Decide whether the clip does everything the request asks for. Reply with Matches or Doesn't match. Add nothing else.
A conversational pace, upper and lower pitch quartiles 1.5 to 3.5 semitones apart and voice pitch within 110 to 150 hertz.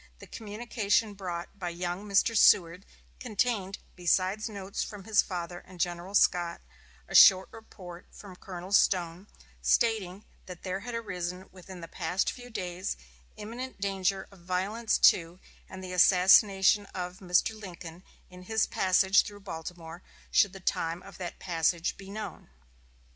Doesn't match